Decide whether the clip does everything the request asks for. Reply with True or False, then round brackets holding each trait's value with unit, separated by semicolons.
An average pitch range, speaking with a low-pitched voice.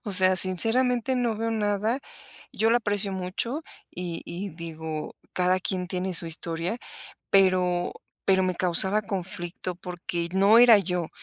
False (3.2 semitones; 185 Hz)